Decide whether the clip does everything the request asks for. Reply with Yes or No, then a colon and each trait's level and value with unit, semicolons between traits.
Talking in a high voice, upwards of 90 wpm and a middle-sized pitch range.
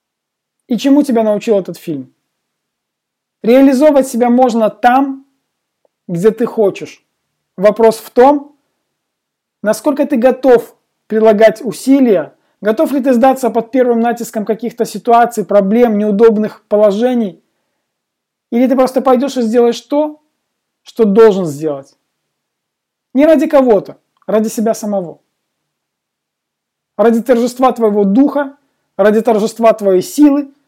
Yes: high, 230 Hz; slow, 110 wpm; average, 3.8 semitones